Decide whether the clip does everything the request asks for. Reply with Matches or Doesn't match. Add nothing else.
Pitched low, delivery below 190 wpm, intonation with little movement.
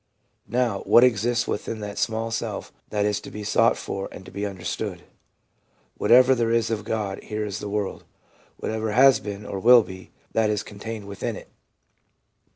Matches